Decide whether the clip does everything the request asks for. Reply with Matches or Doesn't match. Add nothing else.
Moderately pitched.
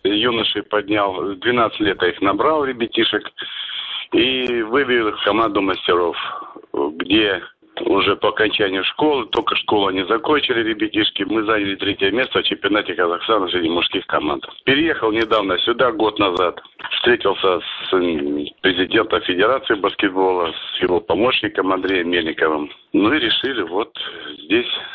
Doesn't match